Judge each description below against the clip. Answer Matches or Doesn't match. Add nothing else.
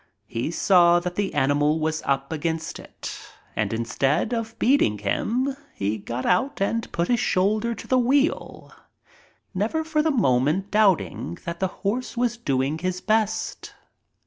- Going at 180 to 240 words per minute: Doesn't match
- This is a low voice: Doesn't match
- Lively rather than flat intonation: Matches